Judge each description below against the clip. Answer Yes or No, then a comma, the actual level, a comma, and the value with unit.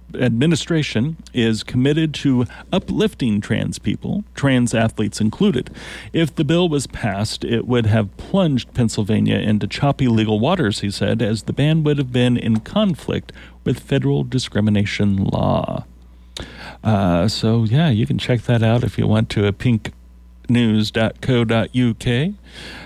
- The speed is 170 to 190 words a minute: No, average, 140 wpm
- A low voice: Yes, low, 115 Hz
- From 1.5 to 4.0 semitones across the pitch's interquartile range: No, average, 4.5 semitones